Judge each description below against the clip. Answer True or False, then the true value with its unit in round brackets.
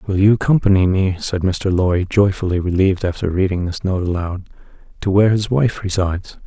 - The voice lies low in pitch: True (95 Hz)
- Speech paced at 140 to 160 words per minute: False (175 wpm)